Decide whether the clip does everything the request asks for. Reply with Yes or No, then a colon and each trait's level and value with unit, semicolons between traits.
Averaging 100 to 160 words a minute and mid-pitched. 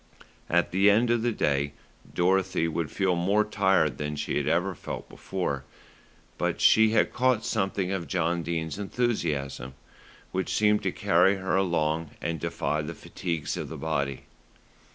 No: average, 155 wpm; very low, 90 Hz